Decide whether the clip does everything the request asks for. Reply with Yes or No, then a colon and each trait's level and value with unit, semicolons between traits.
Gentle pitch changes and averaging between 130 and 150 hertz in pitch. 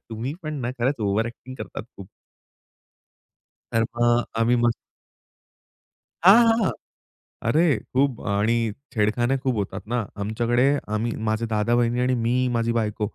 No: narrow, 2.2 semitones; low, 120 Hz